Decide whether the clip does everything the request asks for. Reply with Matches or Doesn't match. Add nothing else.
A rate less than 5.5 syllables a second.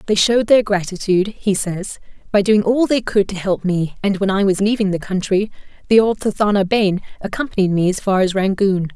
Doesn't match